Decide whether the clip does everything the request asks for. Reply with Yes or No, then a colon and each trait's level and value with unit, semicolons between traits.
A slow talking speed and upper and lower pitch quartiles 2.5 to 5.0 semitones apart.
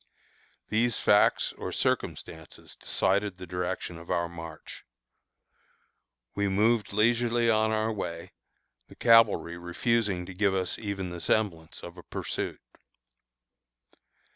Yes: slow, 115 wpm; average, 4.0 semitones